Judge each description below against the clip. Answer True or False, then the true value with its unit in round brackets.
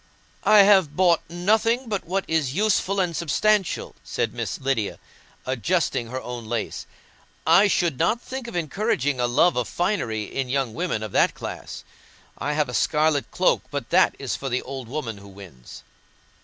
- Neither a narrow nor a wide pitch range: False (7.2 semitones)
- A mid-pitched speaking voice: True (150 Hz)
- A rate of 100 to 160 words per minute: False (170 wpm)